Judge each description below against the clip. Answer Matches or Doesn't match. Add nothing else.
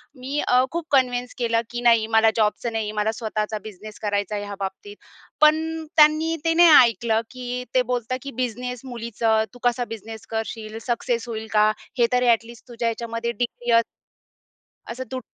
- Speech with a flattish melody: Matches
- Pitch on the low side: Doesn't match